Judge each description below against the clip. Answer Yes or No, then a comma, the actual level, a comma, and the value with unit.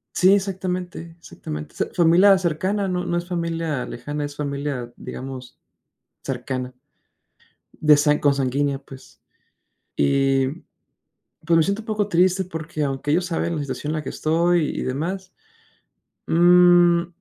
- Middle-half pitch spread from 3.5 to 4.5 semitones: Yes, average, 4.2 semitones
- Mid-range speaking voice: Yes, medium, 165 Hz